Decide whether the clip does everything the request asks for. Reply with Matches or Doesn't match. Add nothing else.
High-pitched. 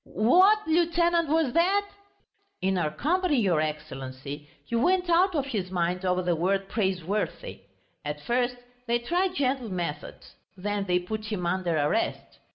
Matches